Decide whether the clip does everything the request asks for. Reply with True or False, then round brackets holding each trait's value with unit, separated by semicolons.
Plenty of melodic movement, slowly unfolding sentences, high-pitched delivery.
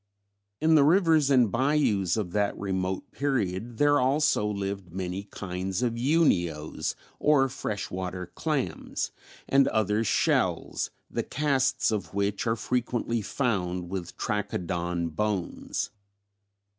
False (6.3 semitones; 120 wpm; 105 Hz)